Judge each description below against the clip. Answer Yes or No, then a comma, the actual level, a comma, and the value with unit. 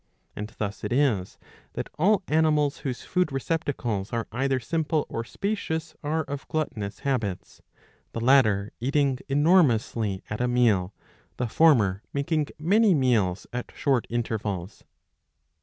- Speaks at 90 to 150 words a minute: Yes, slow, 135 wpm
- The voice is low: Yes, low, 130 Hz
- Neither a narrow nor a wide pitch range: No, wide, 5.9 semitones